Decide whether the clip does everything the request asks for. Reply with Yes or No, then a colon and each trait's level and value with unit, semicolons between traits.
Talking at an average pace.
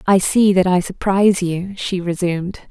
Yes: average, 180 wpm